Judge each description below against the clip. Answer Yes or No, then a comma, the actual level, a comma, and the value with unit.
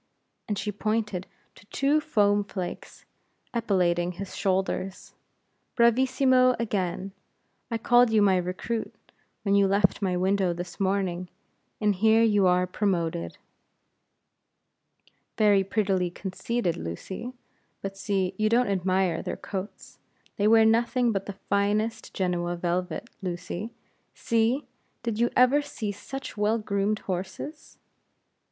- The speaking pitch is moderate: No, high, 200 Hz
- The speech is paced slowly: Yes, slow, 120 wpm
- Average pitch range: Yes, average, 3.4 semitones